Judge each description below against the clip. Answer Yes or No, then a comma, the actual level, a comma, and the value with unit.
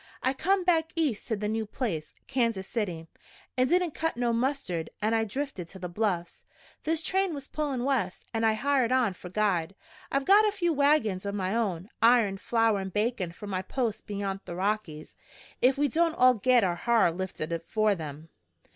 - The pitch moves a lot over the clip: Yes, wide, 6.1 semitones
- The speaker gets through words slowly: No, average, 190 wpm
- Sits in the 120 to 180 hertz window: No, high, 225 Hz